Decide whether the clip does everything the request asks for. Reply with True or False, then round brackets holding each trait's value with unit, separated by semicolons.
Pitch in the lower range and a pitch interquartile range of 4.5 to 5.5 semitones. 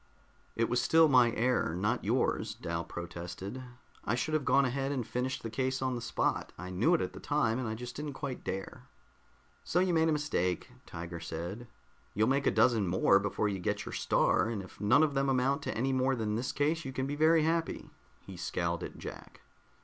True (125 Hz; 5.0 semitones)